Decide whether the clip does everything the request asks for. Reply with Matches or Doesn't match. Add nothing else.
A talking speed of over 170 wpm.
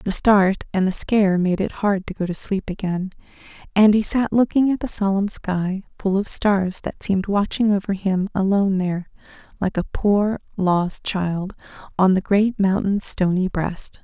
Matches